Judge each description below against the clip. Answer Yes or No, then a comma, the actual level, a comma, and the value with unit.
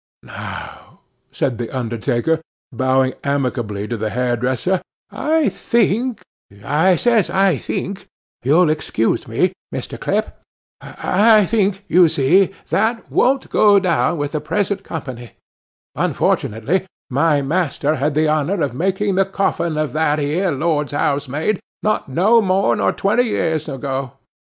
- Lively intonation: Yes, wide, 6.4 semitones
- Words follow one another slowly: Yes, slow, 130 wpm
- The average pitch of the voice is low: No, medium, 160 Hz